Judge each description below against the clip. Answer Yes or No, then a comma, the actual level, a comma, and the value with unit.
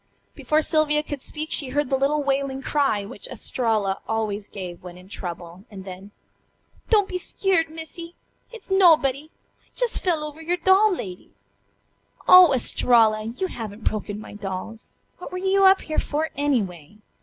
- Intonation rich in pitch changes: Yes, wide, 7.7 semitones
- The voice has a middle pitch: No, very high, 275 Hz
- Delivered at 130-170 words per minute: Yes, average, 160 wpm